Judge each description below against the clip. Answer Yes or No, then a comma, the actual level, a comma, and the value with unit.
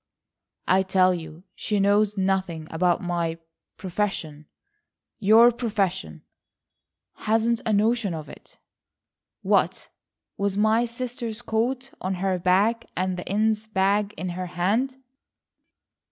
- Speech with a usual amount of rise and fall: Yes, average, 3.5 semitones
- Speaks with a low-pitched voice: No, high, 195 Hz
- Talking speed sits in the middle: No, slow, 110 wpm